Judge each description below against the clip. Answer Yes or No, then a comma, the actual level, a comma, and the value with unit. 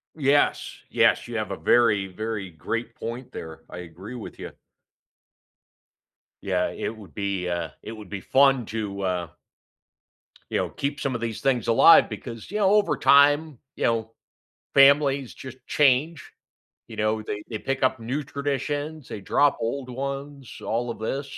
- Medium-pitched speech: No, low, 120 Hz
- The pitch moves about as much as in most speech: Yes, average, 4.7 semitones